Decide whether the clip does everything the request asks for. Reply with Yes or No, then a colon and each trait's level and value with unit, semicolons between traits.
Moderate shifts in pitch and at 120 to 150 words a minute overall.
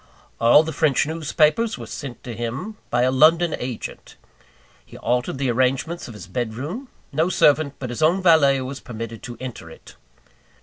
No: average, 4.7 semitones; average, 175 wpm